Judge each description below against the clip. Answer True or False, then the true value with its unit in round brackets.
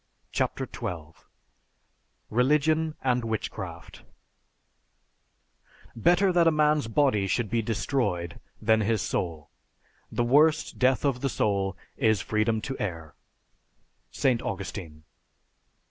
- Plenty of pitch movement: True (6.2 semitones)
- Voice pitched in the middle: False (115 Hz)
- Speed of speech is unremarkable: False (105 wpm)